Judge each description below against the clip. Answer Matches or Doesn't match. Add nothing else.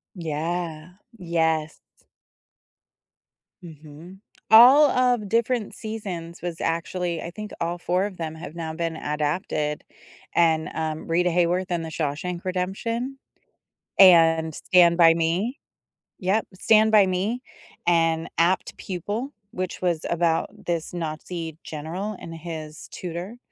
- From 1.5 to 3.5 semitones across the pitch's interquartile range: Matches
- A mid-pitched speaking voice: Matches